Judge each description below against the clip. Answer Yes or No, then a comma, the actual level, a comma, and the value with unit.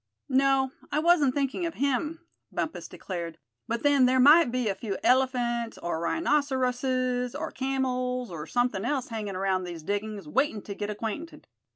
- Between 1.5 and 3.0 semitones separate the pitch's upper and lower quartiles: No, average, 4.6 semitones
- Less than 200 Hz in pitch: No, very high, 250 Hz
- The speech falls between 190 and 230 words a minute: No, average, 160 wpm